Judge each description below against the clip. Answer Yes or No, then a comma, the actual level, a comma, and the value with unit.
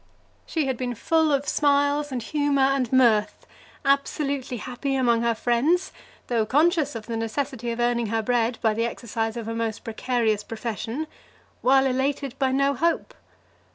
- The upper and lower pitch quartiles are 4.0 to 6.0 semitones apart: No, average, 3.5 semitones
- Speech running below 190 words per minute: Yes, average, 160 wpm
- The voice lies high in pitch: Yes, very high, 250 Hz